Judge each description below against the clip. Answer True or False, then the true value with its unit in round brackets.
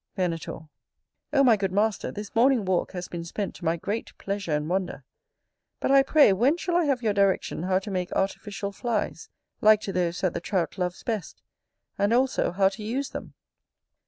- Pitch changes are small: False (3.9 semitones)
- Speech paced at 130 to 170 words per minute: False (190 wpm)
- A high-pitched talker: True (200 Hz)